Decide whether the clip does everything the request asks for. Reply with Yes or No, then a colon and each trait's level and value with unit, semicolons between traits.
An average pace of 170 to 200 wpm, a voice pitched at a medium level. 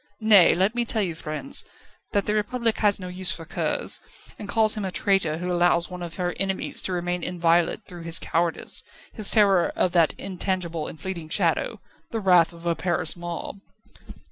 Yes: average, 190 wpm; medium, 180 Hz